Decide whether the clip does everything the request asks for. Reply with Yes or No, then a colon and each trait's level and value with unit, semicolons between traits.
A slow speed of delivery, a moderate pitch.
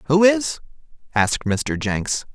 Yes: slow, 130 wpm; medium, 145 Hz